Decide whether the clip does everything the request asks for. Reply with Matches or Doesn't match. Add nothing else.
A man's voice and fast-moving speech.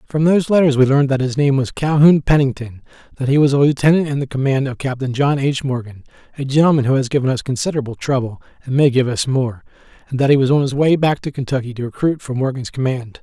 Matches